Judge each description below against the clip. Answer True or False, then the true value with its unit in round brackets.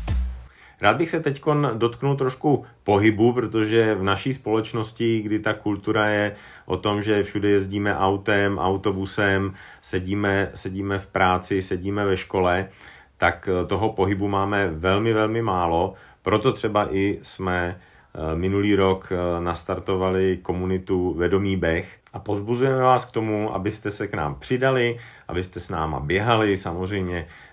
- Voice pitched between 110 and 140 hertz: False (100 Hz)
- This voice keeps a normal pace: True (135 wpm)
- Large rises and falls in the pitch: False (2.9 semitones)